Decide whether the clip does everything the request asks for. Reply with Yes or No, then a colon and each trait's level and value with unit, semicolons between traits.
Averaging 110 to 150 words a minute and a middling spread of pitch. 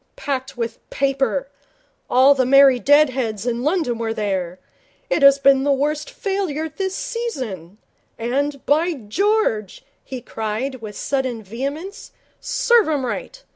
Yes: slow, 135 wpm; average, 4.8 semitones